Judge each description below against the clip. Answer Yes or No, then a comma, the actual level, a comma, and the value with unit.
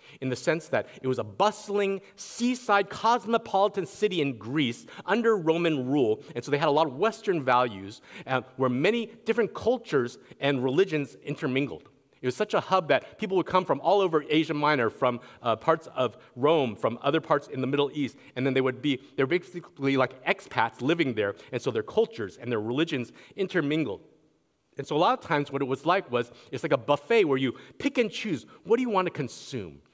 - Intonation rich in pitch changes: Yes, wide, 7.4 semitones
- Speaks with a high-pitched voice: No, medium, 155 Hz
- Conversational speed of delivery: No, fast, 210 wpm